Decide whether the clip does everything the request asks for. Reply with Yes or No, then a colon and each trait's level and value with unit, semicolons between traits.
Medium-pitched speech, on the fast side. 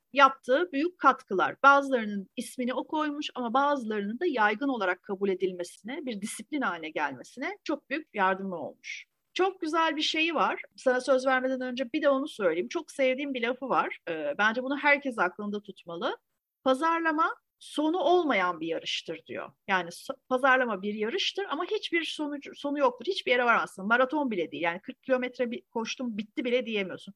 No: very high, 265 Hz; fast, 165 wpm